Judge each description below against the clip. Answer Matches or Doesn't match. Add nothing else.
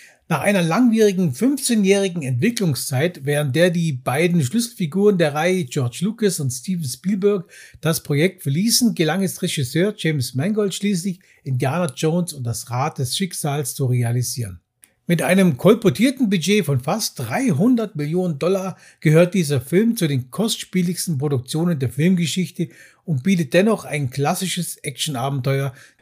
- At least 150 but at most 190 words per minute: Doesn't match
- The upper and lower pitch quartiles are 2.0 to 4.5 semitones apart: Doesn't match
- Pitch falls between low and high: Matches